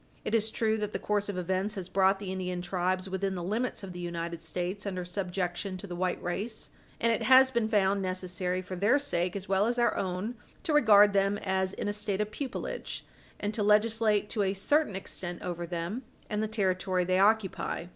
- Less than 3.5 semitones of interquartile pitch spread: Yes, narrow, 2.5 semitones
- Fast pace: Yes, fast, 210 wpm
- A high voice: Yes, high, 195 Hz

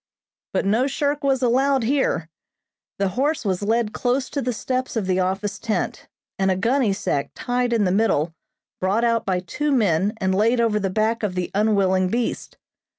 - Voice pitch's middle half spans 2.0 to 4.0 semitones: No, average, 4.6 semitones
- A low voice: No, high, 220 Hz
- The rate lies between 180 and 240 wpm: Yes, average, 185 wpm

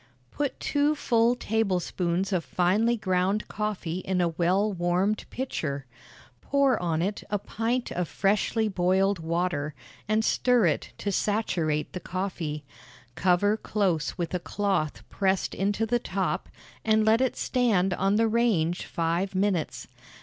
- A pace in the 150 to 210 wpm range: No, average, 140 wpm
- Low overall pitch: No, high, 195 Hz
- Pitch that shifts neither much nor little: Yes, average, 3.7 semitones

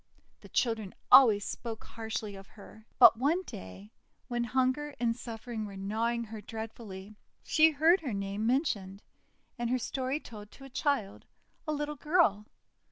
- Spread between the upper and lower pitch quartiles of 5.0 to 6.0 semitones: No, average, 4.3 semitones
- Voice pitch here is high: Yes, high, 230 Hz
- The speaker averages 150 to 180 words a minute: Yes, average, 160 wpm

